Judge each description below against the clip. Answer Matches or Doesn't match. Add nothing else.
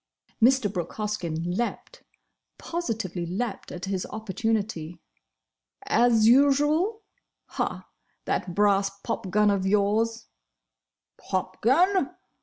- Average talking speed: Doesn't match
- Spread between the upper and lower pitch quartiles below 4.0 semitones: Doesn't match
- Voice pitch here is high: Matches